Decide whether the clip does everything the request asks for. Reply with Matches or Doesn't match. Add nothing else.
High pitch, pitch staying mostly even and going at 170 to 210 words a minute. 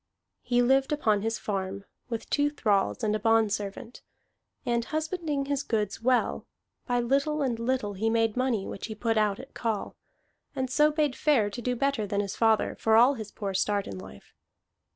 Doesn't match